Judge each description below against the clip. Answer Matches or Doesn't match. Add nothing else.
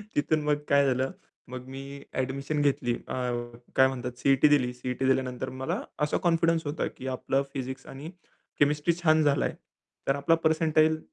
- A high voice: Doesn't match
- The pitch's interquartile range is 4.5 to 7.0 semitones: Doesn't match